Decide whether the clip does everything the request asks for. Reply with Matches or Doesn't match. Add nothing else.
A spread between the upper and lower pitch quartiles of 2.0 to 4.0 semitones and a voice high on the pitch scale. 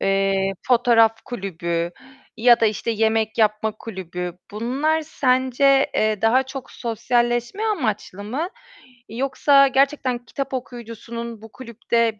Matches